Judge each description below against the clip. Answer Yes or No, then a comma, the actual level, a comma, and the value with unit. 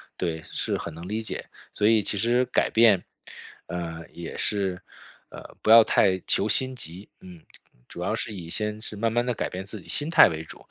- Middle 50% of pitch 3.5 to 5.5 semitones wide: Yes, average, 4.3 semitones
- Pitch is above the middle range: No, low, 100 Hz